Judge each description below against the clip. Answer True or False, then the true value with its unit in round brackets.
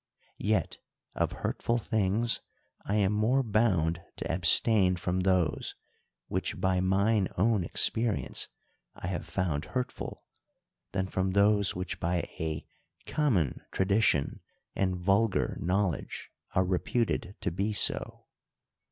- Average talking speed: False (115 wpm)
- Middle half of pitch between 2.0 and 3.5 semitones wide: True (2.9 semitones)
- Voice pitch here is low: True (95 Hz)